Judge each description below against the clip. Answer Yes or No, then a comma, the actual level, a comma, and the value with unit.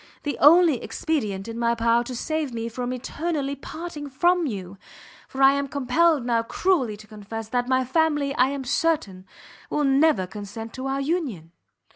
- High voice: Yes, very high, 260 Hz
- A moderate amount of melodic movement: Yes, average, 4.7 semitones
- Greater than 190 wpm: No, average, 170 wpm